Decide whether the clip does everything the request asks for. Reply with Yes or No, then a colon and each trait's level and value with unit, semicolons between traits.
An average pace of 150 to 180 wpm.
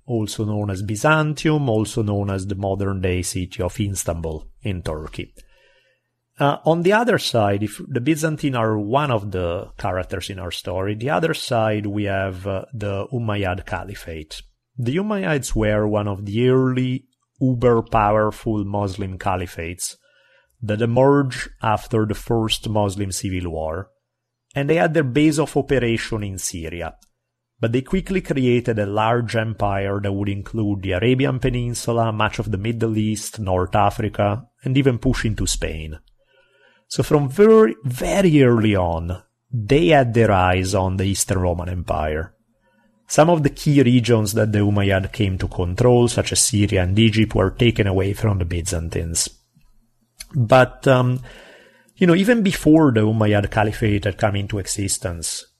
Yes: average, 155 wpm